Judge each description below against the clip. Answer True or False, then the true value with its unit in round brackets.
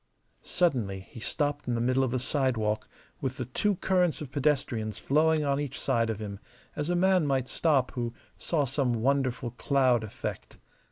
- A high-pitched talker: False (130 Hz)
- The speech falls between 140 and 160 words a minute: False (175 wpm)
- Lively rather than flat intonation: False (3.8 semitones)